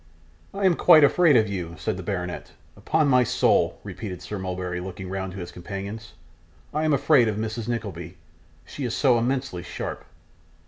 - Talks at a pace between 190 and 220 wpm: No, average, 175 wpm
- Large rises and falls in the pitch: Yes, wide, 5.9 semitones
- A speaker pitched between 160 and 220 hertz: No, low, 110 Hz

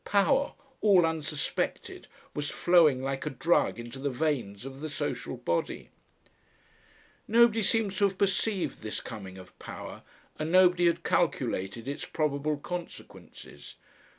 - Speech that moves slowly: Yes, slow, 130 wpm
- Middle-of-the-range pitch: Yes, medium, 155 Hz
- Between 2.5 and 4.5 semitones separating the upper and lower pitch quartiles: No, wide, 5.6 semitones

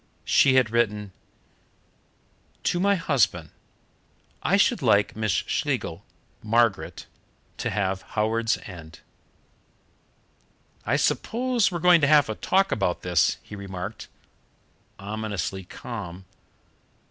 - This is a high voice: No, low, 110 Hz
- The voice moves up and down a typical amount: No, wide, 6.2 semitones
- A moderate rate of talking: No, slow, 105 wpm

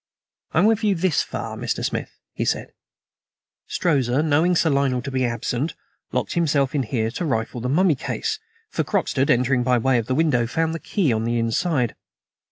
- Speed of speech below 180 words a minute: No, average, 185 wpm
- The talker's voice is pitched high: No, low, 135 Hz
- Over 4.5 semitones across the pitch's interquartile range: Yes, average, 5.0 semitones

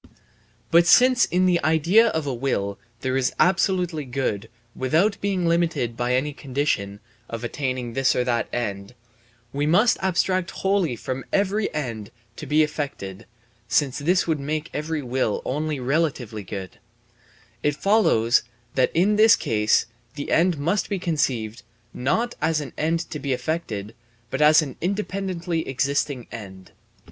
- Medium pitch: Yes, medium, 150 Hz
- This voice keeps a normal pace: Yes, average, 150 wpm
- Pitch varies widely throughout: Yes, wide, 5.8 semitones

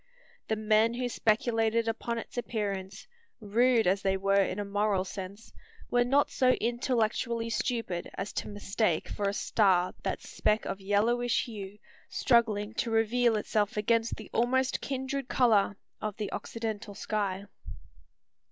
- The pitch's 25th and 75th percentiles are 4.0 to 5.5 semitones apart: No, average, 2.7 semitones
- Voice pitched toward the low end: No, high, 220 Hz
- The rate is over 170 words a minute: No, average, 145 wpm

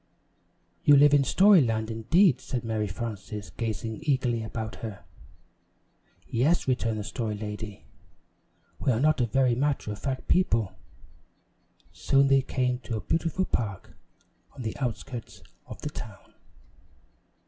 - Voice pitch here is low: Yes, low, 120 Hz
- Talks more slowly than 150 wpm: Yes, slow, 135 wpm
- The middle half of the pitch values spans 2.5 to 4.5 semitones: Yes, average, 3.9 semitones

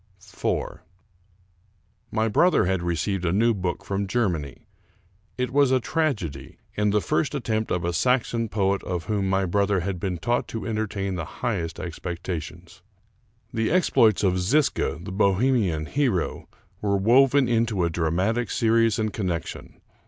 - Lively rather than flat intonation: No, average, 4.4 semitones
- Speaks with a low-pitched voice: Yes, low, 100 Hz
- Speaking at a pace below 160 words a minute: Yes, average, 150 wpm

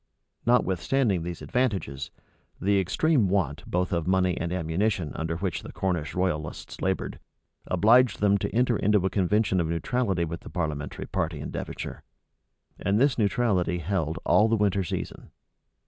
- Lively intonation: No, average, 3.8 semitones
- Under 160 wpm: Yes, average, 150 wpm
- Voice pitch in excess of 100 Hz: No, very low, 95 Hz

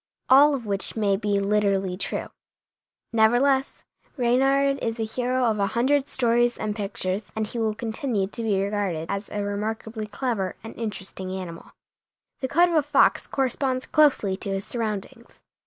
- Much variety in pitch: No, average, 4.2 semitones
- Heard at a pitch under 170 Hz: No, high, 220 Hz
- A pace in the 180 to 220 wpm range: No, average, 160 wpm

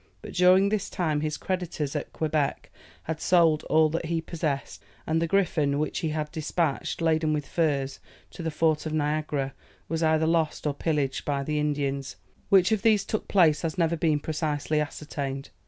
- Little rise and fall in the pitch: Yes, narrow, 2.1 semitones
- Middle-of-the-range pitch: Yes, medium, 155 Hz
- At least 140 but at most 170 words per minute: No, average, 180 wpm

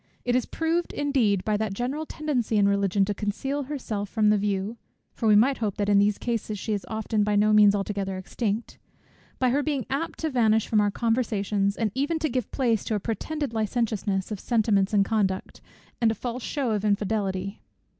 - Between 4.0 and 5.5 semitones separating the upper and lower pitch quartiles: No, average, 3.4 semitones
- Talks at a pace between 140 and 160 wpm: No, average, 200 wpm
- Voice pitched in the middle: No, high, 215 Hz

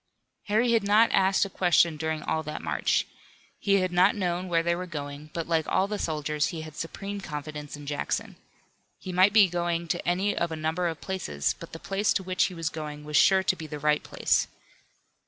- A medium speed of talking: No, fast, 215 wpm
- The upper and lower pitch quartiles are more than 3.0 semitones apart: Yes, average, 3.6 semitones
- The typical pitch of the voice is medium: Yes, medium, 170 Hz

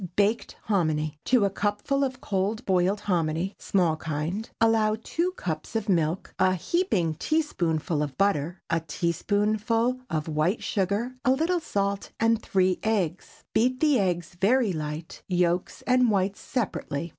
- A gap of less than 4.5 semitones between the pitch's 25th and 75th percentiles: No, average, 5.1 semitones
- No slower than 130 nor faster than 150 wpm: Yes, average, 145 wpm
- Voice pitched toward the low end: No, high, 195 Hz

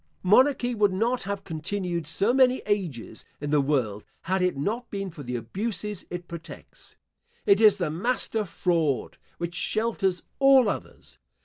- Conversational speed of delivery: Yes, average, 155 wpm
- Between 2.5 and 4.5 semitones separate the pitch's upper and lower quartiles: No, average, 5.0 semitones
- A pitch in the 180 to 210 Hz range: Yes, high, 190 Hz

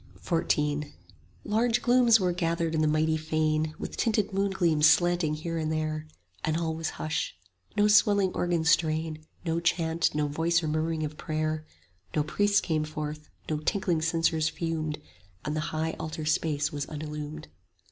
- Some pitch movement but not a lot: No, narrow, 1.8 semitones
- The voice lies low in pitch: No, medium, 160 Hz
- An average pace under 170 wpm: Yes, average, 160 wpm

